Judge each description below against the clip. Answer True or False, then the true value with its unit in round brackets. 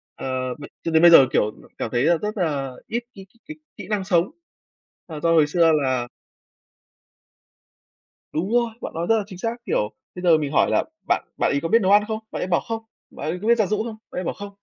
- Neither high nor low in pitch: True (175 Hz)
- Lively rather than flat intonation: True (5.9 semitones)